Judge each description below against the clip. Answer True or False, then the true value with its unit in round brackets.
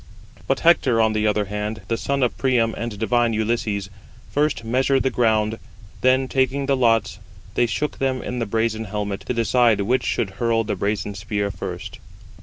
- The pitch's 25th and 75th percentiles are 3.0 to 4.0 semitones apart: True (3.4 semitones)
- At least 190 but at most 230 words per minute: False (180 wpm)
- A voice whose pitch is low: True (115 Hz)